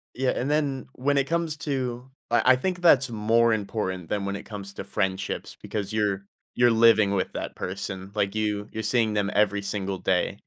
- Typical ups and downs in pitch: Yes, average, 4.1 semitones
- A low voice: Yes, low, 110 Hz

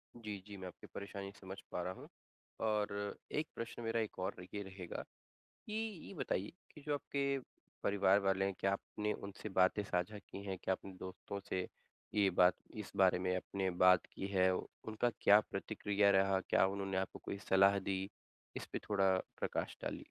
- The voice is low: Yes, low, 100 Hz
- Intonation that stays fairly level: Yes, narrow, 1.8 semitones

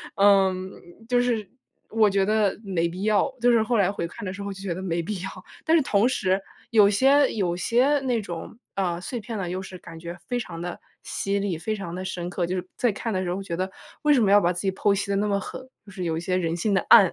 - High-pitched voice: Yes, high, 195 Hz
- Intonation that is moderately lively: Yes, average, 3.3 semitones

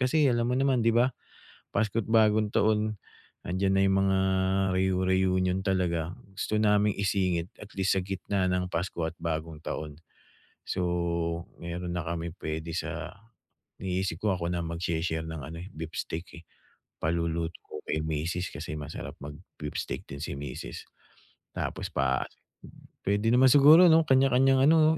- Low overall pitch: Yes, very low, 90 Hz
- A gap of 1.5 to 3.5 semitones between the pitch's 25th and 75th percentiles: No, average, 4.3 semitones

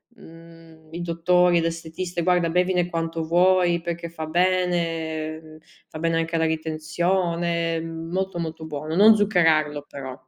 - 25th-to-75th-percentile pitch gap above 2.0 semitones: No, narrow, 1.7 semitones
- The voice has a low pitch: No, medium, 165 Hz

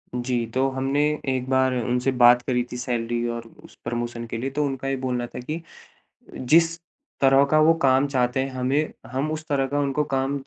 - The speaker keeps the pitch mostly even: Yes, narrow, 2.0 semitones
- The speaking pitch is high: No, low, 130 Hz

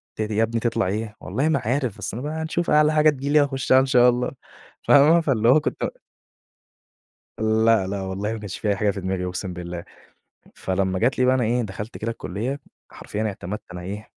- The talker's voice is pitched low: Yes, low, 110 Hz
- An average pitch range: Yes, average, 5.0 semitones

